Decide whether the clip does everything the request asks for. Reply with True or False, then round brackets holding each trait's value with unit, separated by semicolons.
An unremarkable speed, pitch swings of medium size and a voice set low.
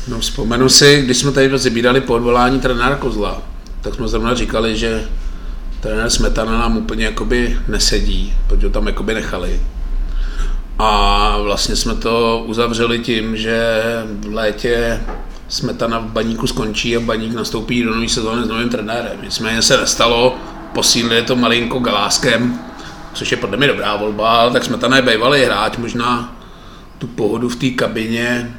False (155 wpm; 1.5 semitones; 115 Hz)